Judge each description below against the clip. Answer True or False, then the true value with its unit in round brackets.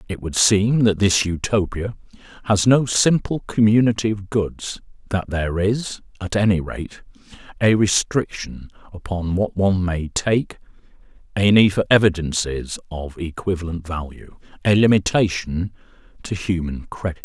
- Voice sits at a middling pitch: False (95 Hz)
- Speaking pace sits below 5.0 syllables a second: True (4.5 syllables/s)